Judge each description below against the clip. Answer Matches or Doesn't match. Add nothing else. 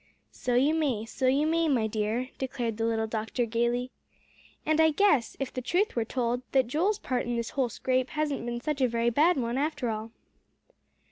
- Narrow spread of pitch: Doesn't match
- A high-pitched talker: Matches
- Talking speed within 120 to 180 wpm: Doesn't match